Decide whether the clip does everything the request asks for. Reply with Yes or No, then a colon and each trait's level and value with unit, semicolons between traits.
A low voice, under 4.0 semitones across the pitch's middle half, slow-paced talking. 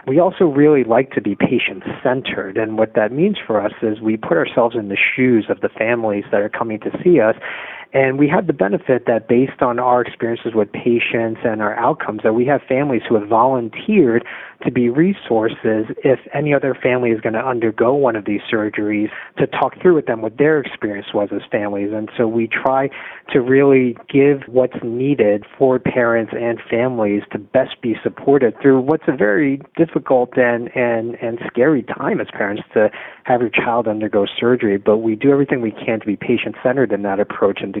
No: low, 120 Hz; average, 3.4 semitones; fast, 205 wpm